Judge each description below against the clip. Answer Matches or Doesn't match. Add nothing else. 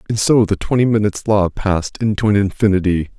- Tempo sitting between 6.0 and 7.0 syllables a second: Matches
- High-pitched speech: Doesn't match